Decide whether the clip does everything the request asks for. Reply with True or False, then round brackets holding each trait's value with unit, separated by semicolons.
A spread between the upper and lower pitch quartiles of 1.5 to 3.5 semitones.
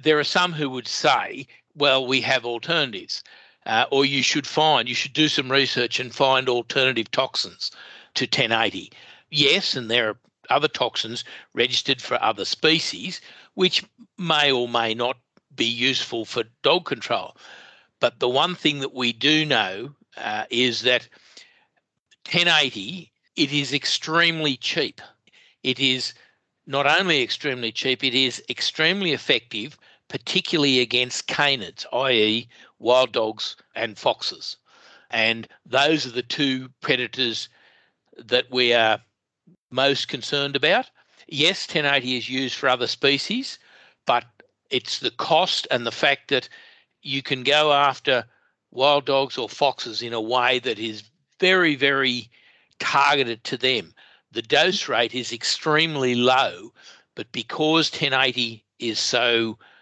True (3.2 semitones)